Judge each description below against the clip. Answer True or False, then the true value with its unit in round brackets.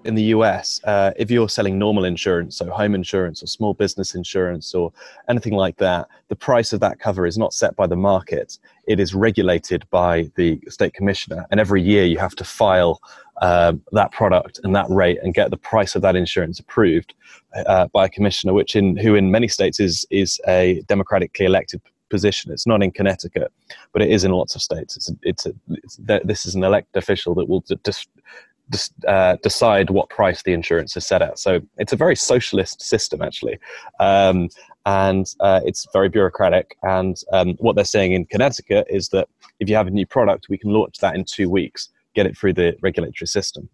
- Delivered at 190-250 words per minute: True (205 wpm)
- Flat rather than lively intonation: True (2.3 semitones)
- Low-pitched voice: True (95 Hz)